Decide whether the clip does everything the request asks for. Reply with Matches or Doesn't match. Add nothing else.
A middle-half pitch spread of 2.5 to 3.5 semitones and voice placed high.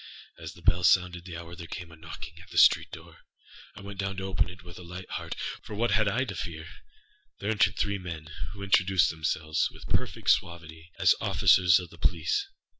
Doesn't match